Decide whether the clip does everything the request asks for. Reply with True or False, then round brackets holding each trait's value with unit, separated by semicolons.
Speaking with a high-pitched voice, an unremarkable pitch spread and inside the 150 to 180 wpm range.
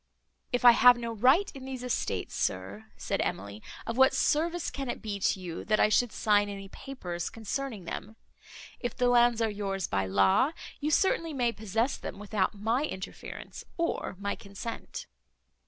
True (225 Hz; 4.7 semitones; 170 wpm)